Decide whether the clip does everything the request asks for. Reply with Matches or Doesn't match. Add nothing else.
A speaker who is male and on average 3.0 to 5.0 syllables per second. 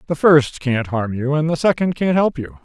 Matches